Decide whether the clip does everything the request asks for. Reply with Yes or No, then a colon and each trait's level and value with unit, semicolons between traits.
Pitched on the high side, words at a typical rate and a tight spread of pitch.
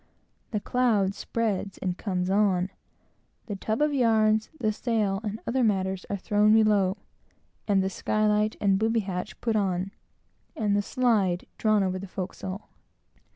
Yes: high, 205 Hz; average, 155 wpm; narrow, 2.3 semitones